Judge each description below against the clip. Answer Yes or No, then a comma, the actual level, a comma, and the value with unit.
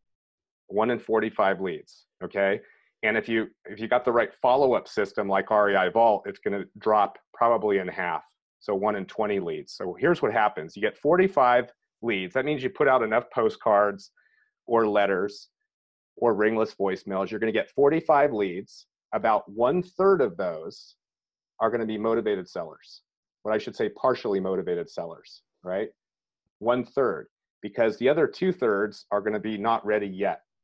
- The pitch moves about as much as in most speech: No, wide, 5.8 semitones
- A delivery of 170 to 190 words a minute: Yes, average, 175 wpm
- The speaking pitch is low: Yes, low, 110 Hz